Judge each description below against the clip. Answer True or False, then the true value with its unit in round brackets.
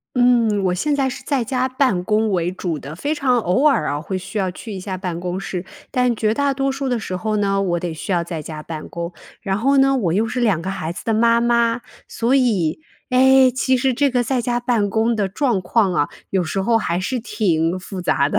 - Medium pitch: False (215 Hz)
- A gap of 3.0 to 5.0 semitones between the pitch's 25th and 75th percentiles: False (5.6 semitones)